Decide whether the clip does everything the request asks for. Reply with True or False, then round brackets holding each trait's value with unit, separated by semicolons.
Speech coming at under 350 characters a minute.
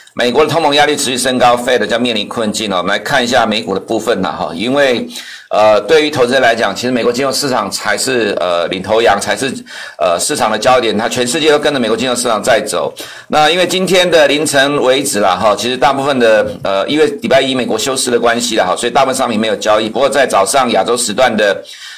False (365 characters per minute)